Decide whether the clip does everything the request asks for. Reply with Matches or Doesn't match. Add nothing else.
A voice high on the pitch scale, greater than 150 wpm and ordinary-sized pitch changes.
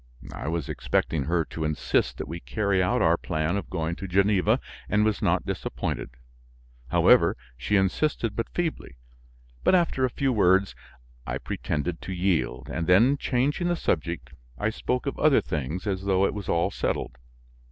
Doesn't match